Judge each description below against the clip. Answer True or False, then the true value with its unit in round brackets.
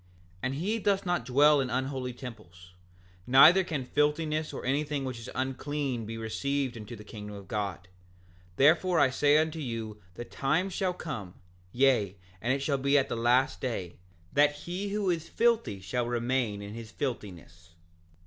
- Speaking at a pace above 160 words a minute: True (170 wpm)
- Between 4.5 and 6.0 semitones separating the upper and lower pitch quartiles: True (4.9 semitones)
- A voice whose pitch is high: False (130 Hz)